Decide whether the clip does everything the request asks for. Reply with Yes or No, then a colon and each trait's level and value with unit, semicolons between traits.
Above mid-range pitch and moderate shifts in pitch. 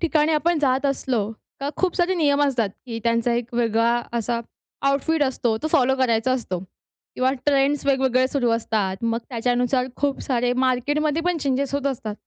Yes: very high, 260 Hz; average, 3.3 semitones